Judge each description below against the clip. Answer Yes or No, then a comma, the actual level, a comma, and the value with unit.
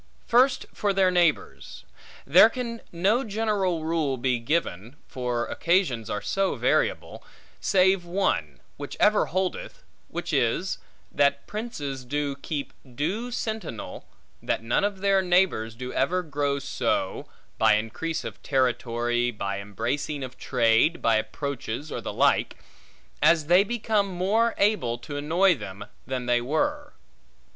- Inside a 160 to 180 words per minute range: No, slow, 135 wpm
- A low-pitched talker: No, medium, 155 Hz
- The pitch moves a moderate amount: No, wide, 7.9 semitones